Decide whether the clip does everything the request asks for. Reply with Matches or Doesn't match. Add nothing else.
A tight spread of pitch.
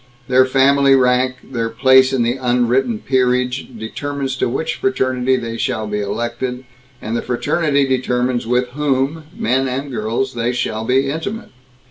Matches